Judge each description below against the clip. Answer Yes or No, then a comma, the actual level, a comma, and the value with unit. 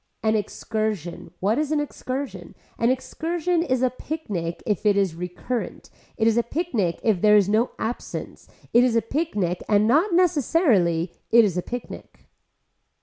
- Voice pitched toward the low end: No, high, 225 Hz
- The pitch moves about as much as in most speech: No, wide, 5.9 semitones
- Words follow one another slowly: No, average, 160 wpm